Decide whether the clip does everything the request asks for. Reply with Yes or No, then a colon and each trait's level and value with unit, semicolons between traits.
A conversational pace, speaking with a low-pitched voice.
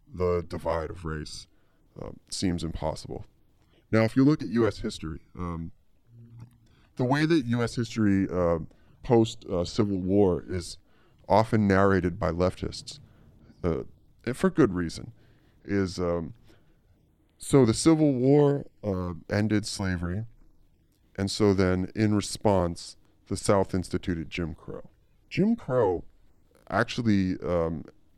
No: slow, 120 wpm; low, 100 Hz